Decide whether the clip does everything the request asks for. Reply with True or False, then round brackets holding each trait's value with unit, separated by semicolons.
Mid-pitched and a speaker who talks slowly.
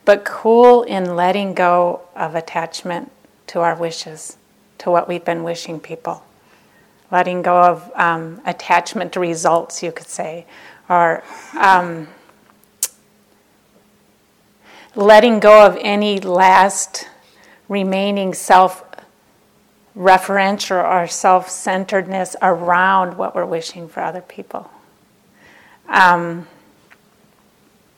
True (180 Hz; 100 wpm)